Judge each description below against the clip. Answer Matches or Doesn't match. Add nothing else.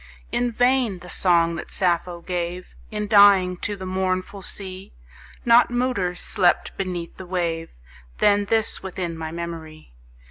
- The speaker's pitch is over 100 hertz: Matches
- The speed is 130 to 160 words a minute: Matches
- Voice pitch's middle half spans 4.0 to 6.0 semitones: Doesn't match